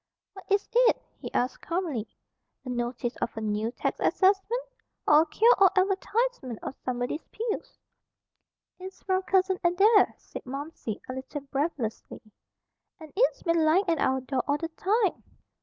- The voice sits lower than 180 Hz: No, very high, 330 Hz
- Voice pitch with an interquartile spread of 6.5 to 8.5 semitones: Yes, wide, 7.1 semitones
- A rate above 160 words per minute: No, average, 155 wpm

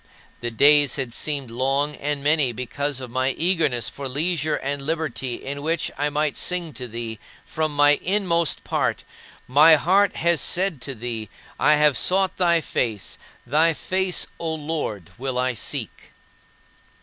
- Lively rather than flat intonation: No, average, 4.0 semitones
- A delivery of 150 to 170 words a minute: Yes, average, 155 wpm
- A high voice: No, medium, 145 Hz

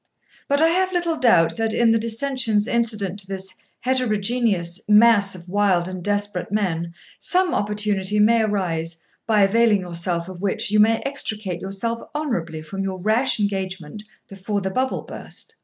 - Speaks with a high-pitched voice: Yes, high, 205 Hz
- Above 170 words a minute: No, average, 155 wpm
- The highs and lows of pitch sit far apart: No, average, 3.6 semitones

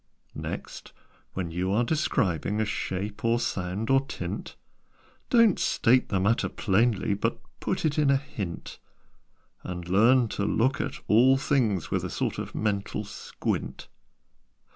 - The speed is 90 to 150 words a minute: Yes, average, 140 wpm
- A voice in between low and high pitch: No, low, 110 Hz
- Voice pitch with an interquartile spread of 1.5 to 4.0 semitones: No, average, 5.2 semitones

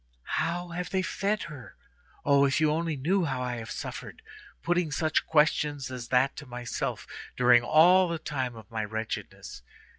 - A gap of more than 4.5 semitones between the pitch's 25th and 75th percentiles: Yes, average, 5.2 semitones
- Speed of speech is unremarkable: Yes, average, 170 wpm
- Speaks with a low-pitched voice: No, medium, 145 Hz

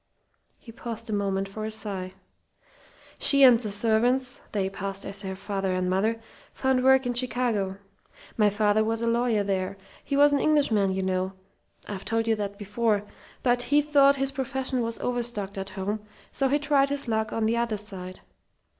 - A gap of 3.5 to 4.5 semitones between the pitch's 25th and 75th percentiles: Yes, average, 4.1 semitones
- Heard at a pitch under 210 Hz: No, high, 220 Hz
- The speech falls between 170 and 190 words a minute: Yes, average, 180 wpm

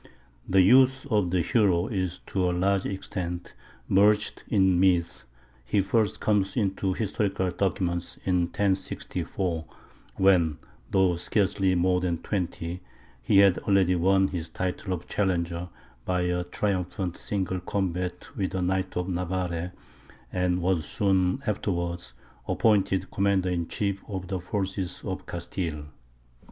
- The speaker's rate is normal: No, slow, 130 wpm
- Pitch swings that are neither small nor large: No, narrow, 1.8 semitones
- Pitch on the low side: Yes, very low, 95 Hz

